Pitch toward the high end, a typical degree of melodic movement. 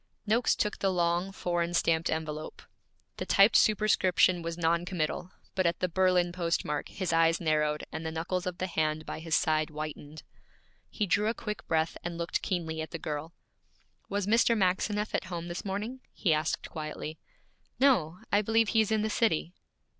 No: medium, 175 Hz; average, 3.6 semitones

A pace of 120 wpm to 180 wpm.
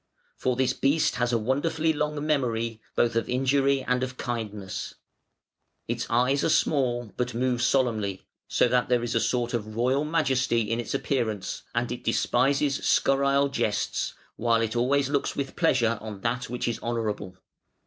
Yes: average, 165 wpm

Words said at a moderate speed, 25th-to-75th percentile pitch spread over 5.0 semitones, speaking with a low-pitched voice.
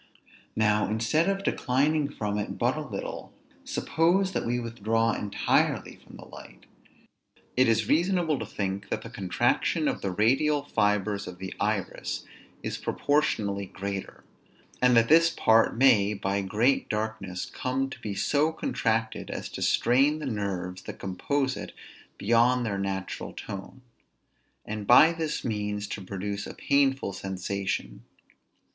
Yes: average, 145 wpm; wide, 5.4 semitones; low, 110 Hz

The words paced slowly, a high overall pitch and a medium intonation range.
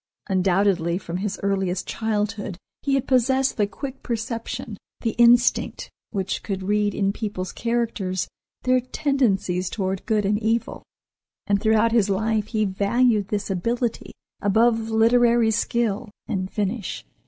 Yes: slow, 130 wpm; high, 215 Hz; average, 3.1 semitones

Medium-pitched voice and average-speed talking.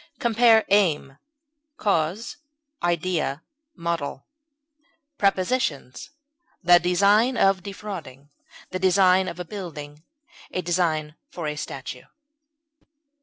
No: medium, 175 Hz; slow, 90 wpm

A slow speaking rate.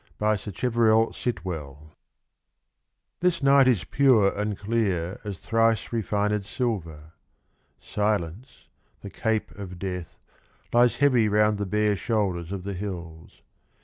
Yes: slow, 125 wpm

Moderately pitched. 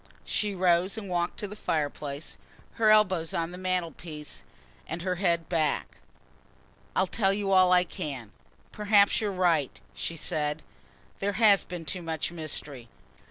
Yes: medium, 175 Hz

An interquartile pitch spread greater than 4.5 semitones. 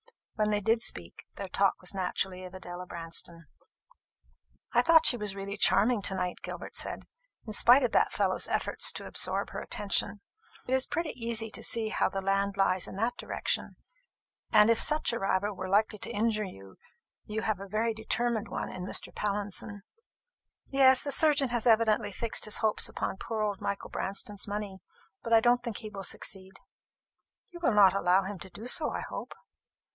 No: average, 3.0 semitones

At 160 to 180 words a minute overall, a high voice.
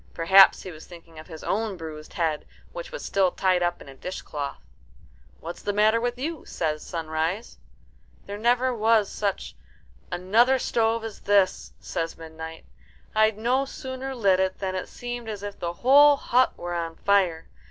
Yes: average, 170 wpm; high, 200 Hz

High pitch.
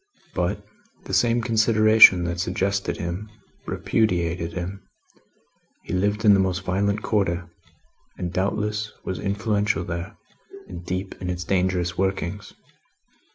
No: very low, 95 Hz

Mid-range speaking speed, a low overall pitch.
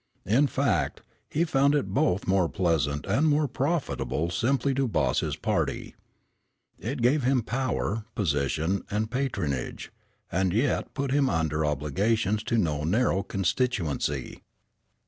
No: slow, 130 wpm; low, 110 Hz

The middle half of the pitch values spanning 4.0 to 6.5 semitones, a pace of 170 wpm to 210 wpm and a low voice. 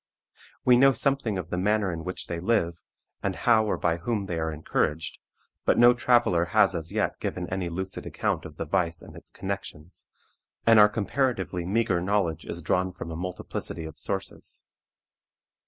Yes: average, 4.3 semitones; average, 175 wpm; very low, 95 Hz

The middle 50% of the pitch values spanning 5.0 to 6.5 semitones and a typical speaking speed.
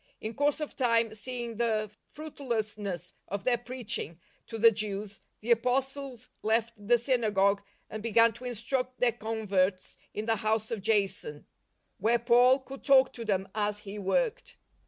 No: average, 3.1 semitones; average, 165 wpm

